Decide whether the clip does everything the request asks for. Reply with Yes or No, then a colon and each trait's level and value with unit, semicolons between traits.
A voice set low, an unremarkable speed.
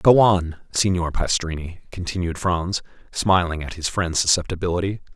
No: very low, 90 Hz; slow, 130 wpm